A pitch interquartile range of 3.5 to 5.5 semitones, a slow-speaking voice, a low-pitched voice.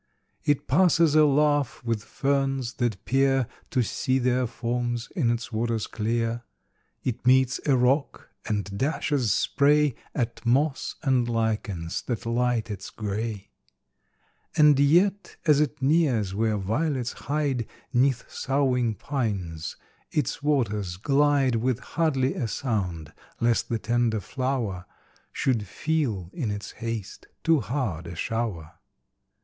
Yes: average, 4.1 semitones; slow, 125 wpm; low, 120 Hz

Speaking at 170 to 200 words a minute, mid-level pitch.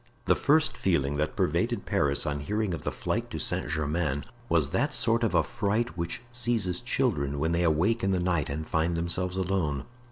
No: average, 190 wpm; very low, 85 Hz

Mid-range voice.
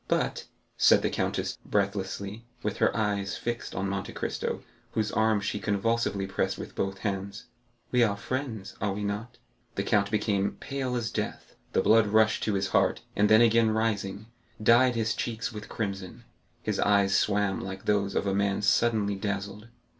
No: low, 105 Hz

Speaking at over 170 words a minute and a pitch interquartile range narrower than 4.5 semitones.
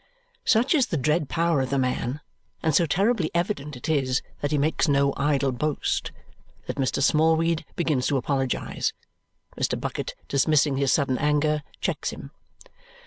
No: average, 155 wpm; average, 2.8 semitones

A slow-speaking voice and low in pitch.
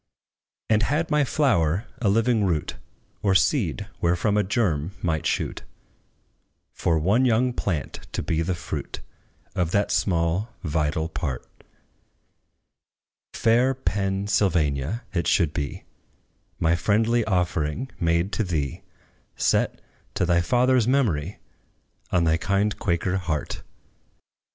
Yes: slow, 120 wpm; very low, 95 Hz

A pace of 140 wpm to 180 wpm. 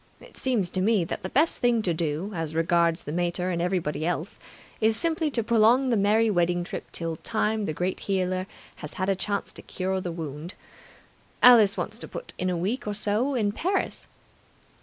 No: average, 200 wpm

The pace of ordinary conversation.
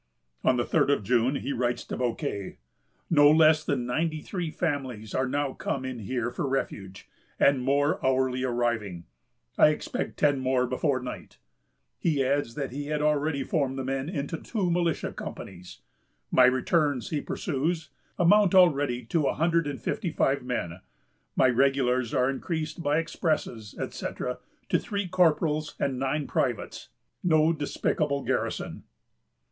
Yes: average, 150 wpm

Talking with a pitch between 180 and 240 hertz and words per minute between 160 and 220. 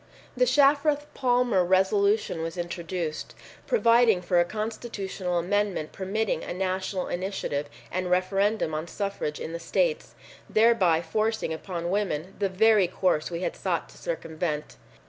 No: high, 190 Hz; slow, 135 wpm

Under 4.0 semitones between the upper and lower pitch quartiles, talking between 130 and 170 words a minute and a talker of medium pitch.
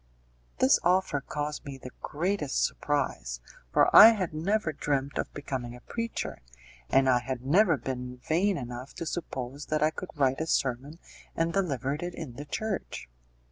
No: average, 4.4 semitones; average, 165 wpm; medium, 145 Hz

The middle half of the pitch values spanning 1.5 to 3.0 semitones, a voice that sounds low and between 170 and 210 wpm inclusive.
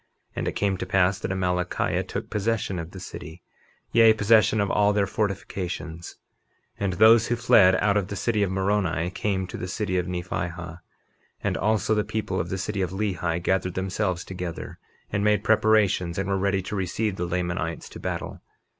Yes: narrow, 2.6 semitones; very low, 95 Hz; average, 190 wpm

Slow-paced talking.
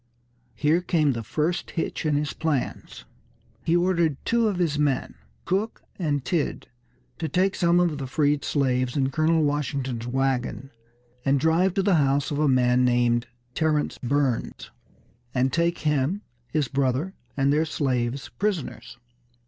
No: average, 150 wpm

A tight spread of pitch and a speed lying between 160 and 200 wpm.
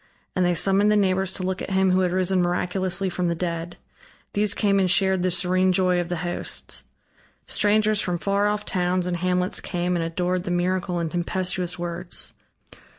Yes: narrow, 1.4 semitones; average, 190 wpm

